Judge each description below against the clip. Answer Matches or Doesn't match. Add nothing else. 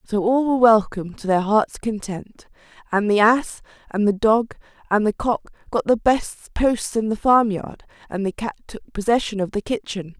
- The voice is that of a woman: Matches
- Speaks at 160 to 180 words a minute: Doesn't match